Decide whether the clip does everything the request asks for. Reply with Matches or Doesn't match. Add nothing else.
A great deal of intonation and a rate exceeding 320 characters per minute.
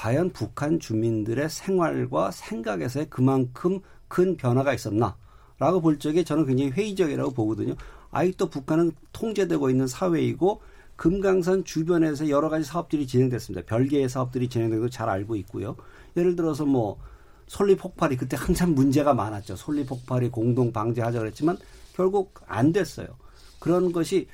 Matches